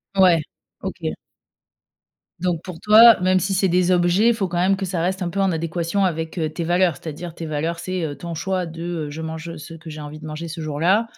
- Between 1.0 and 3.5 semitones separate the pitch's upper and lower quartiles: Yes, narrow, 2.5 semitones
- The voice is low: No, medium, 170 Hz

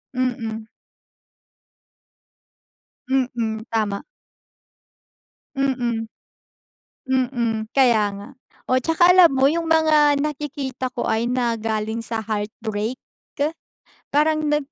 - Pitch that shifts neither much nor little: Yes, average, 4.4 semitones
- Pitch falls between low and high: No, very high, 250 Hz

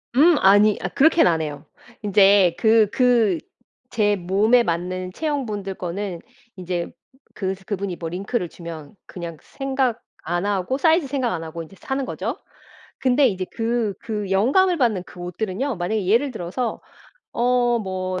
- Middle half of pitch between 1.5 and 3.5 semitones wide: No, wide, 5.4 semitones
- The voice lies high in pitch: Yes, high, 205 Hz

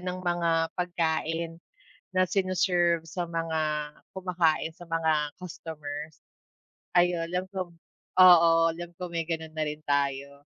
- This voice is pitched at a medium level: Yes, medium, 165 Hz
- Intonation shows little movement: Yes, narrow, 2.0 semitones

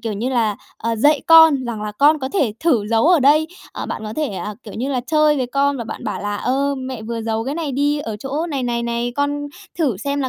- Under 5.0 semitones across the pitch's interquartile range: Yes, average, 4.3 semitones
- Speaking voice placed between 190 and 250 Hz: No, very high, 260 Hz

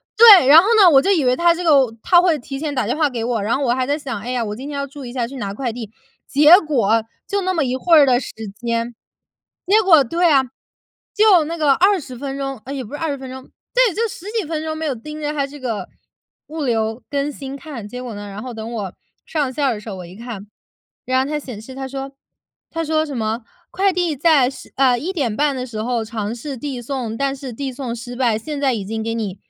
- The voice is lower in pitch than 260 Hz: No, very high, 270 Hz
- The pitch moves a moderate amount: Yes, average, 4.5 semitones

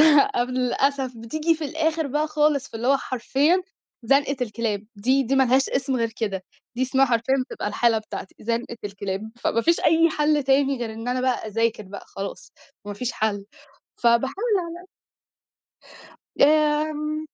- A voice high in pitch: Yes, very high, 260 Hz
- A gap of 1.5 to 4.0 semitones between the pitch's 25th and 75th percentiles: No, average, 4.6 semitones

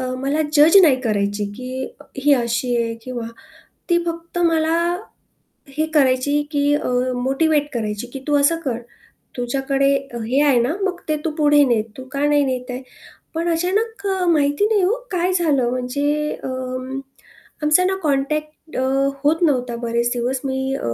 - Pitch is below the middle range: No, very high, 280 Hz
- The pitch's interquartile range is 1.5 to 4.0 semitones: Yes, average, 3.6 semitones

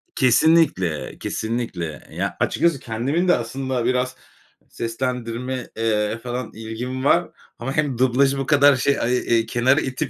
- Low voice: Yes, low, 125 Hz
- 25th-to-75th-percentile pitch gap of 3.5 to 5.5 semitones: No, average, 2.9 semitones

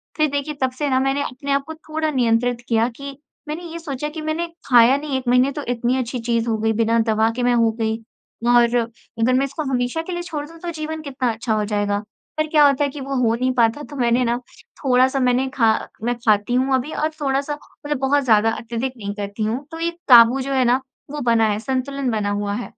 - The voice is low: No, very high, 255 Hz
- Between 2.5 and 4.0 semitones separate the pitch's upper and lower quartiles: Yes, average, 3.6 semitones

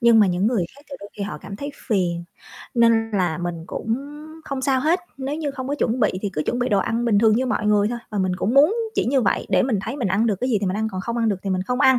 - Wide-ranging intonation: No, average, 4.5 semitones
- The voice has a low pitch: No, high, 225 Hz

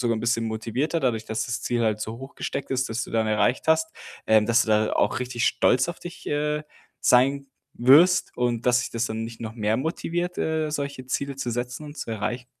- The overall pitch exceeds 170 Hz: No, low, 125 Hz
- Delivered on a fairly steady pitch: No, average, 3.8 semitones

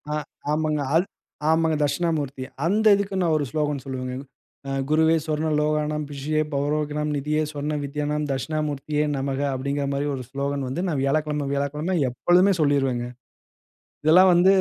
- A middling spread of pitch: No, narrow, 2.0 semitones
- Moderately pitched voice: Yes, medium, 150 Hz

